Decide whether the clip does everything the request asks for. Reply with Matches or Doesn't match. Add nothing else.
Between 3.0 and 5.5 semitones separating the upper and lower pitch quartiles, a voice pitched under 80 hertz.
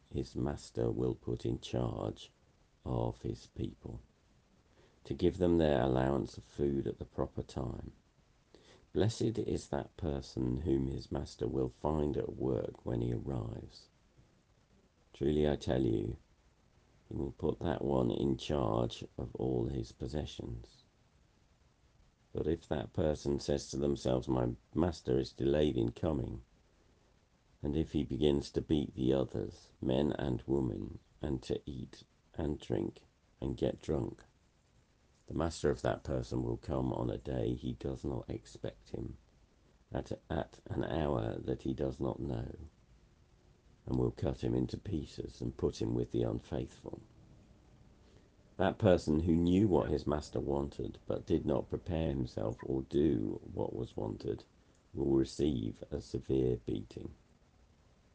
Doesn't match